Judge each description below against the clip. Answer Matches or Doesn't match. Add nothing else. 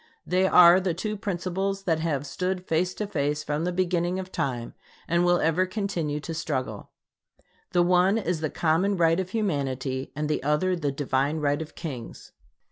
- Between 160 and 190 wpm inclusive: Matches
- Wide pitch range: Doesn't match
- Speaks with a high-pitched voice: Doesn't match